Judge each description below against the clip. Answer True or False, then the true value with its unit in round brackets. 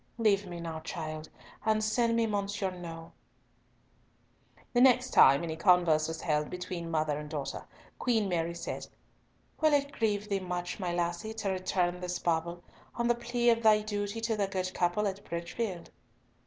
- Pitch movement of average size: True (4.2 semitones)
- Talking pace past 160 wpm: True (170 wpm)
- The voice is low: False (185 Hz)